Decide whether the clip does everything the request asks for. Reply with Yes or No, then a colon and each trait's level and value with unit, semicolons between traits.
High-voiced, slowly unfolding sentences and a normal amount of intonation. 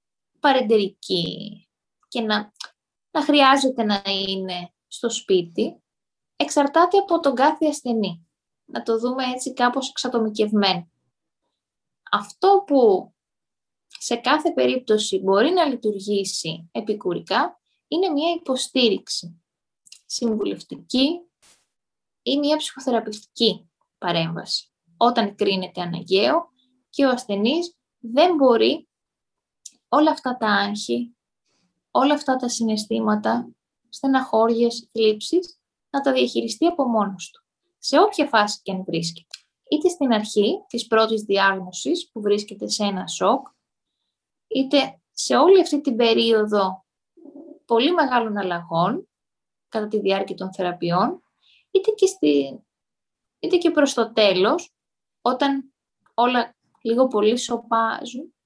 No: high, 230 Hz; slow, 105 wpm; wide, 5.9 semitones